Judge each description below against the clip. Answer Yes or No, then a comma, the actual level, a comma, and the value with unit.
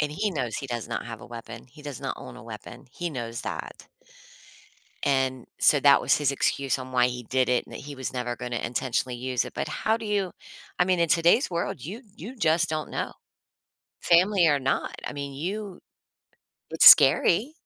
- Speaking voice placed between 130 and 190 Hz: Yes, medium, 140 Hz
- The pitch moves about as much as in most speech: No, wide, 5.7 semitones